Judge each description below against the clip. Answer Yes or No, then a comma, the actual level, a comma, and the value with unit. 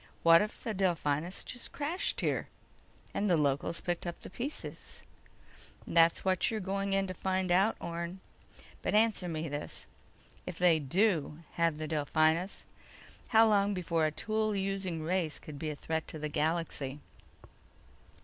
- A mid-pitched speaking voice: Yes, medium, 175 Hz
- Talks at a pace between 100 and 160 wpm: Yes, average, 155 wpm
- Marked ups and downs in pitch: No, average, 3.8 semitones